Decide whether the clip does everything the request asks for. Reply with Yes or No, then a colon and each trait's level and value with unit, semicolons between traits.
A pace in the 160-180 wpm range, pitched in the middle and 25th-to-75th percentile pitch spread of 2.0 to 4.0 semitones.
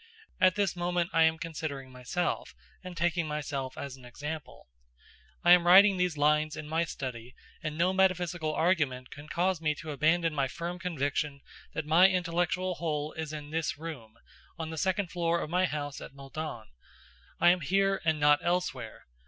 Yes: average, 175 wpm; medium, 160 Hz; average, 3.2 semitones